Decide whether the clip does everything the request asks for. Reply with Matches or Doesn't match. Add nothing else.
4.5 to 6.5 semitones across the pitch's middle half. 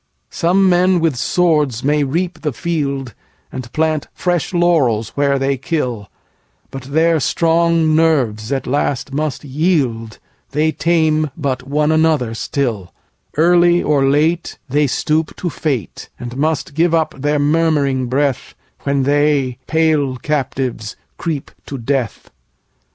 Doesn't match